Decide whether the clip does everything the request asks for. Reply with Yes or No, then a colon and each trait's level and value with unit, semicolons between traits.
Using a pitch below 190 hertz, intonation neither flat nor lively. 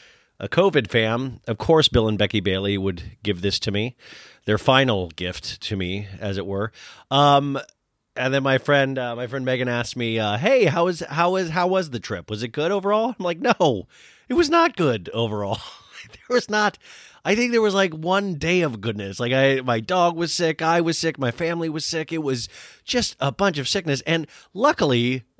No: low, 135 Hz; wide, 7.2 semitones